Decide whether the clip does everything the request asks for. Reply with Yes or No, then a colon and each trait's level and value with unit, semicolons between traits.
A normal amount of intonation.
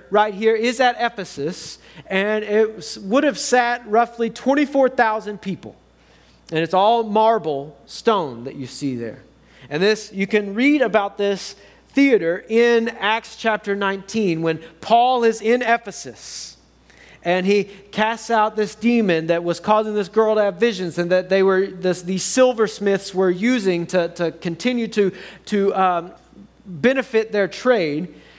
Yes: average, 4.2 semitones